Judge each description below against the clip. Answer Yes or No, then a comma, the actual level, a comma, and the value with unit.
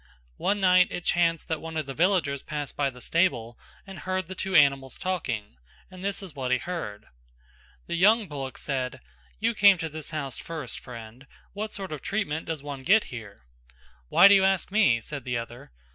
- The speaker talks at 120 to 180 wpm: No, average, 195 wpm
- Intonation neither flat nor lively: No, wide, 6.0 semitones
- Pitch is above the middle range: No, medium, 160 Hz